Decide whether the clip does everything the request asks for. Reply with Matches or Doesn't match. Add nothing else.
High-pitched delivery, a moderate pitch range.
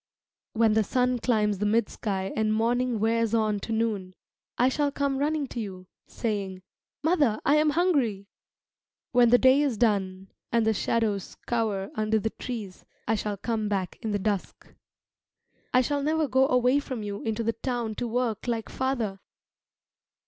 Matches